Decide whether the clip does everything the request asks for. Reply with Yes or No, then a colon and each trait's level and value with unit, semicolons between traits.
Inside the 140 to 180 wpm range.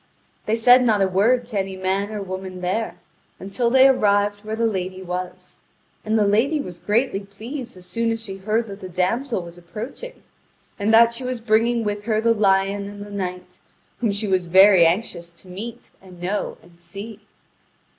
No: average, 190 wpm